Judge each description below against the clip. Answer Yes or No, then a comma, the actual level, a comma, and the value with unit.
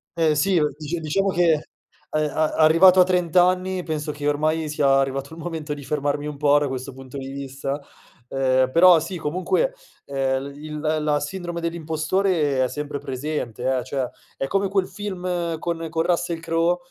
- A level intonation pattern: No, average, 3.4 semitones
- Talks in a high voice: No, medium, 155 Hz